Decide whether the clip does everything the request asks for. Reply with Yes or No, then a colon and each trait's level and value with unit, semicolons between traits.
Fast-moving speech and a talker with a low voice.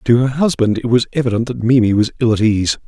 Yes: fast, 250 wpm; low, 120 Hz